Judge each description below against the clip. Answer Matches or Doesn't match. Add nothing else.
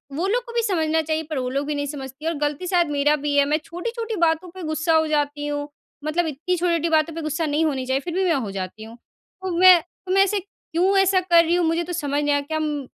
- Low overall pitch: Doesn't match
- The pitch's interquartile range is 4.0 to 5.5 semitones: Doesn't match